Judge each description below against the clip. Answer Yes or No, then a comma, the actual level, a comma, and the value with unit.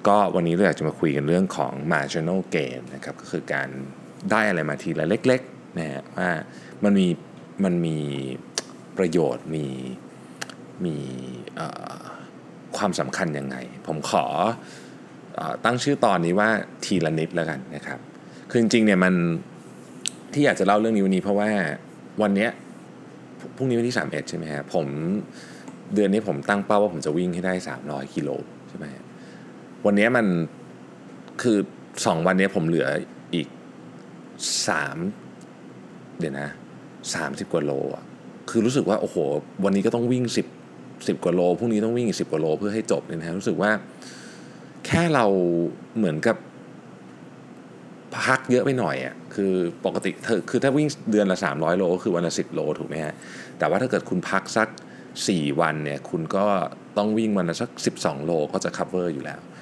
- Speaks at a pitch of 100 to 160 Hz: No, very low, 90 Hz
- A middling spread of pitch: No, wide, 6.2 semitones